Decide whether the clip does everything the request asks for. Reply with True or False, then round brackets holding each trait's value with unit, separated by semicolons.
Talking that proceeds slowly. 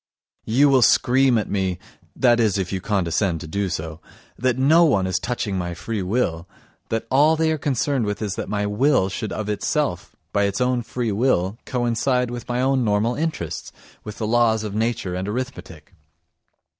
False (185 wpm)